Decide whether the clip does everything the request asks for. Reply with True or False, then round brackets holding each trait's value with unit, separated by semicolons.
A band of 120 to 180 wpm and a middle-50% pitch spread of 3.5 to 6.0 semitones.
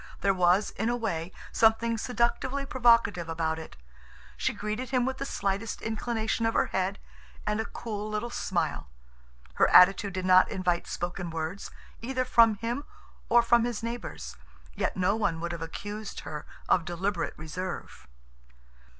True (155 wpm; 4.8 semitones)